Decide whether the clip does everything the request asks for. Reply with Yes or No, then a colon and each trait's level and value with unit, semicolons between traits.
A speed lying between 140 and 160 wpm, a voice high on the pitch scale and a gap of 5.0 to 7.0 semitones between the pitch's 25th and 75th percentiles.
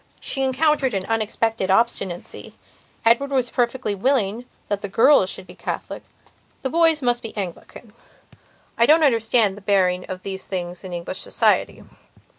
Yes: average, 150 wpm; high, 225 Hz; average, 5.3 semitones